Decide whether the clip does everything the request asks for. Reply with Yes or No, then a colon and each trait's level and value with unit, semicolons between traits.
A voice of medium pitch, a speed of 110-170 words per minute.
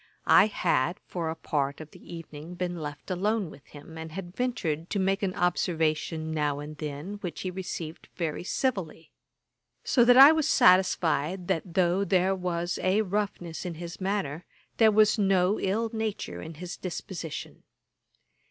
Yes: medium, 180 Hz; average, 160 wpm